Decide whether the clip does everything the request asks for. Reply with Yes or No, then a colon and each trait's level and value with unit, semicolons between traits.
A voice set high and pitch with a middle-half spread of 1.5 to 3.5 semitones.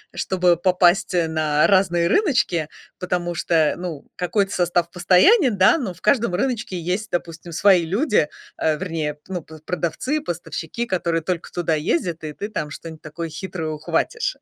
No: medium, 175 Hz; average, 2.8 semitones